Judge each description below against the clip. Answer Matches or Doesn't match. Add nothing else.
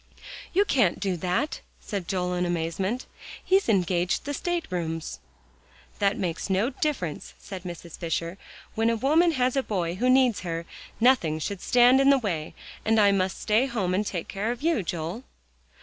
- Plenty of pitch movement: Matches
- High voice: Matches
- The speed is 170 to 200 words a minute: Matches